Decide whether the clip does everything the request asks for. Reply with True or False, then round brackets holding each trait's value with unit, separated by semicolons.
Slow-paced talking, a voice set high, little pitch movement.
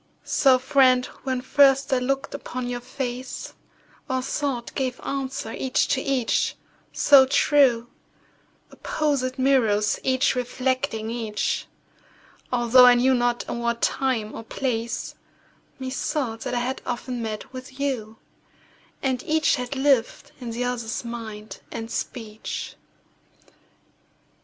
True (125 wpm; 255 Hz; 2.1 semitones)